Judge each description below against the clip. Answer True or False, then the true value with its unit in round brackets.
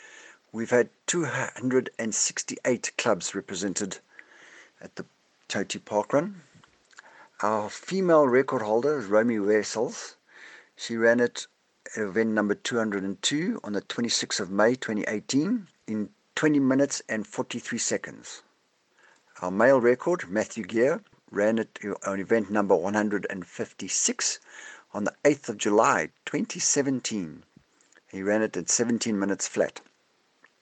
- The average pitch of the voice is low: True (115 Hz)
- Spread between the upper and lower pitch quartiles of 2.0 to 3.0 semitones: False (4.6 semitones)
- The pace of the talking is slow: True (120 wpm)